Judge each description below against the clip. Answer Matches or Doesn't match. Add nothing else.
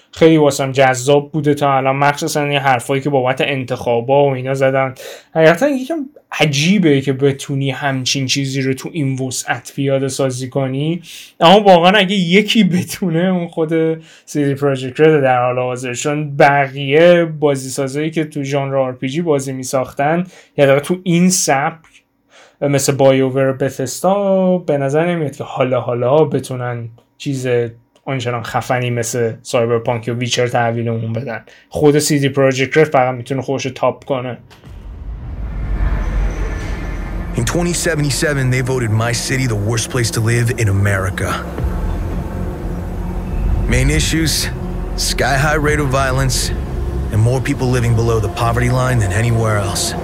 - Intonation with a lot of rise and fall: Doesn't match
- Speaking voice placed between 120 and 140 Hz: Matches